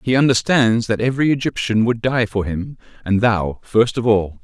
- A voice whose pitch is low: Yes, low, 115 Hz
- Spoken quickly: No, average, 190 wpm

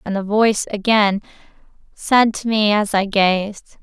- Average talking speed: Yes, average, 155 wpm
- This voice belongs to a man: No, female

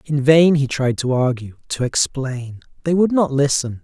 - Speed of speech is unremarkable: Yes, average, 190 wpm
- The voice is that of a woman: No, male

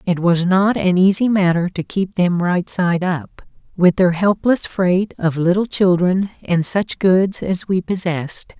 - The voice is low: No, medium, 185 Hz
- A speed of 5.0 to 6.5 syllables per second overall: No, 4.0 syllables/s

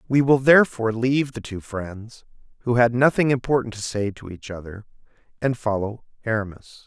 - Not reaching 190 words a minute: Yes, average, 165 wpm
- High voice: No, low, 115 Hz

